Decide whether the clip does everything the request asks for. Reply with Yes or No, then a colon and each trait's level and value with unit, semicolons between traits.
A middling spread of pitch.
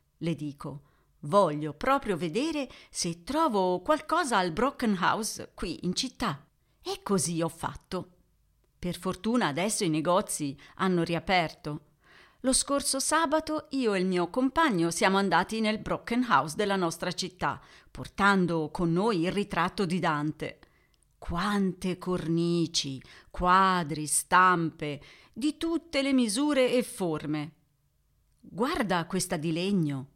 No: wide, 6.0 semitones